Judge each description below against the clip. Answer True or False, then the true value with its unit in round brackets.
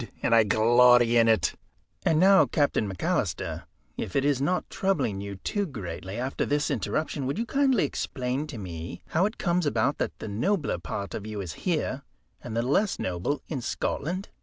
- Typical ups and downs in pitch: False (7.2 semitones)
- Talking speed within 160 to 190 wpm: True (185 wpm)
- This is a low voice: True (130 Hz)